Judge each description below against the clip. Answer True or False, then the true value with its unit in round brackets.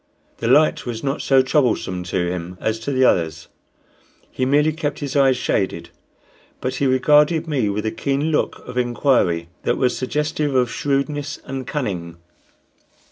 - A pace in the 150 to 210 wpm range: True (160 wpm)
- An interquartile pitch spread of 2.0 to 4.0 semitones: False (5.1 semitones)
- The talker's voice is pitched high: False (130 Hz)